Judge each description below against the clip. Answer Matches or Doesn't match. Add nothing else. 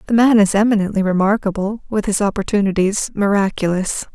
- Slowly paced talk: Matches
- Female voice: Matches